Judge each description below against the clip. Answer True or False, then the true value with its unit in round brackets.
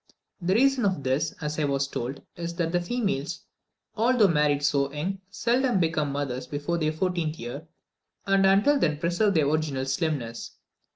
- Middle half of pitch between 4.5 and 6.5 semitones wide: True (5.2 semitones)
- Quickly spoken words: False (165 wpm)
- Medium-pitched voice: True (160 Hz)